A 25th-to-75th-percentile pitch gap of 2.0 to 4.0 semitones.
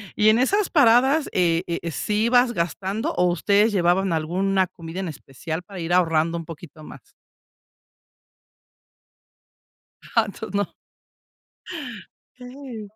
No: average, 4.9 semitones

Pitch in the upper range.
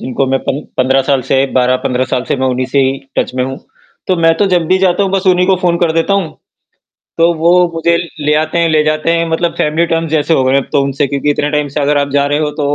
No: medium, 150 Hz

